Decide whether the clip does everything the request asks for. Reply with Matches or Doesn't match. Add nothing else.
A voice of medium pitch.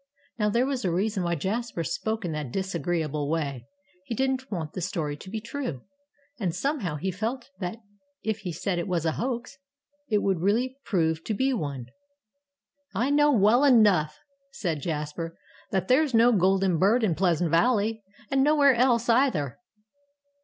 Doesn't match